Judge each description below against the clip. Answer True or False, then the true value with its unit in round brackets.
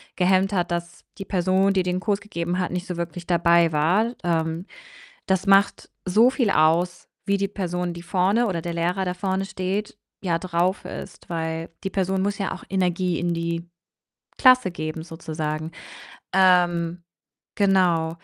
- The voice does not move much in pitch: True (2.3 semitones)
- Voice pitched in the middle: True (180 Hz)